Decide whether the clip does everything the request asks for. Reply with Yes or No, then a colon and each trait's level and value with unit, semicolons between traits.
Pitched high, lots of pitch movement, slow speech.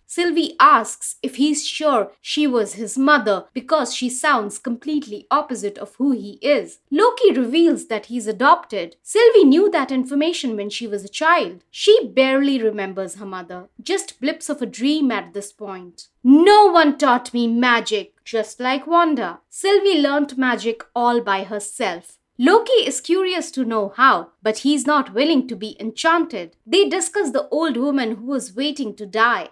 No: very high, 265 Hz; wide, 5.9 semitones; average, 165 wpm